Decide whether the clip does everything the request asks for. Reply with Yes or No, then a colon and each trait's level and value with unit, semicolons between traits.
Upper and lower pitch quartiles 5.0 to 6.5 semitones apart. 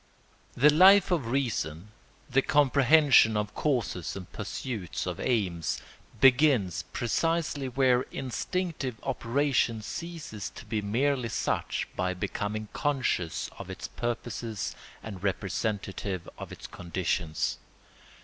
Yes: wide, 5.6 semitones